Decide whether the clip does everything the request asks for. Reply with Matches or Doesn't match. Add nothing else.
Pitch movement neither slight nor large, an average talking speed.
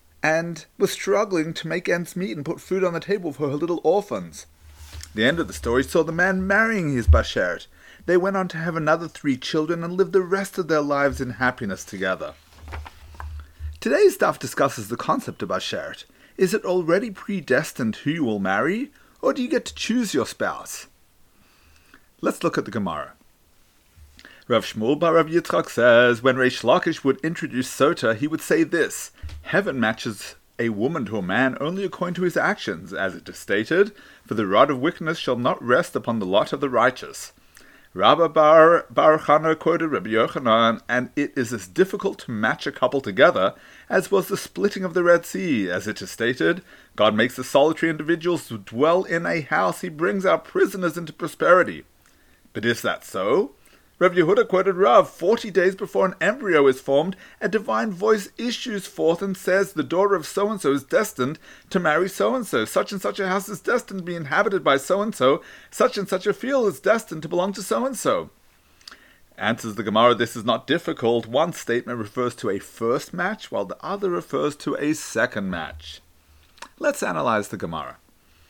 Doesn't match